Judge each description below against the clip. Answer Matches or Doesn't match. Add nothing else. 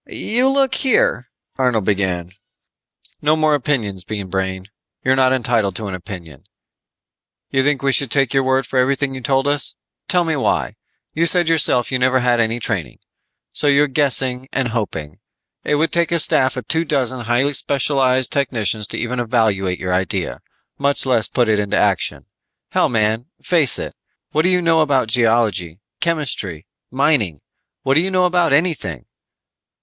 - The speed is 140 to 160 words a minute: Doesn't match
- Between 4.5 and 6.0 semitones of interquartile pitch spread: Matches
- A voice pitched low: Matches